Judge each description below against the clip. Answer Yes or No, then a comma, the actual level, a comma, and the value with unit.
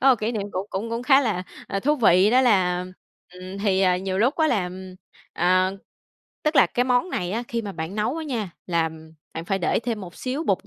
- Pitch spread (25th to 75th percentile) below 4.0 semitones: No, average, 5.2 semitones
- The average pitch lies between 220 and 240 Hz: No, high, 200 Hz